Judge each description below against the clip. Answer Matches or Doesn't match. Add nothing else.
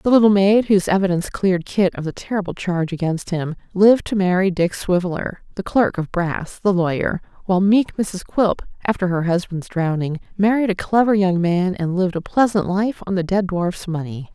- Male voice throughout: Doesn't match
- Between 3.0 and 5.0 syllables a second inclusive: Doesn't match